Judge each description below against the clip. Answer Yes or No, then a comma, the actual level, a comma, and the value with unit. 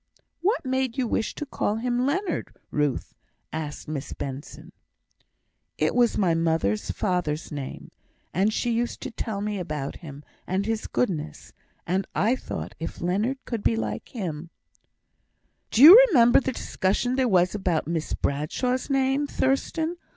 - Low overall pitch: No, high, 205 Hz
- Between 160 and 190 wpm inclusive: No, average, 150 wpm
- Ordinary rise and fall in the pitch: No, wide, 8.1 semitones